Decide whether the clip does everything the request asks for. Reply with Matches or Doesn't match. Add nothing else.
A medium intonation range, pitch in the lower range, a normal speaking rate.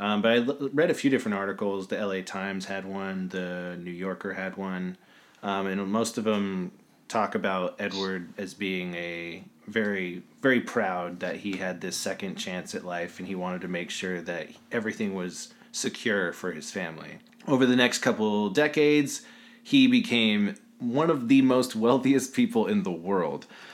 Doesn't match